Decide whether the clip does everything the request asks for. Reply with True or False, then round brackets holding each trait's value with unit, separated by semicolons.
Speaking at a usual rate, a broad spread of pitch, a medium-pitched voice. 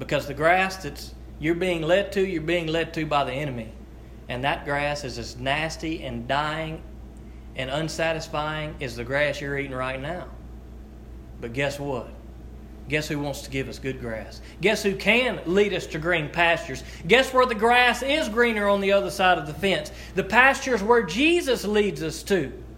True (185 wpm; 6.2 semitones; 160 Hz)